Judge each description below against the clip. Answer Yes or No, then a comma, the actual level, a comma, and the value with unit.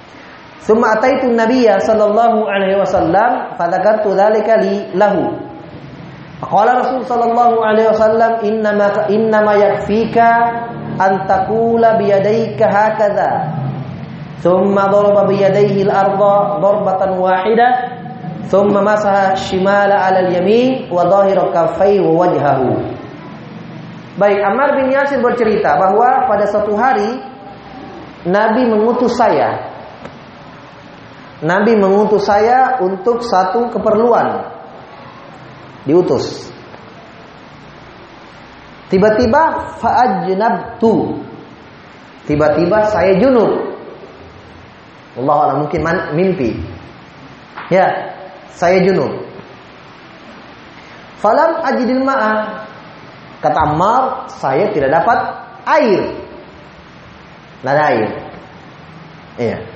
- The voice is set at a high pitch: Yes, high, 205 Hz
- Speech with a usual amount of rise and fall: Yes, average, 3.3 semitones